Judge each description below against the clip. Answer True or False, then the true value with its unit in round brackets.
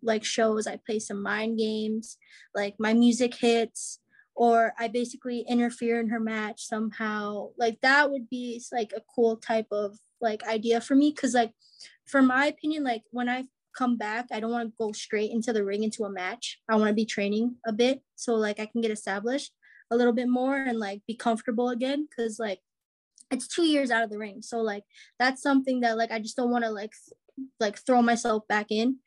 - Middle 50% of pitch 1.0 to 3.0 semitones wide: True (2.4 semitones)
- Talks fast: True (210 wpm)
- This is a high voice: True (230 Hz)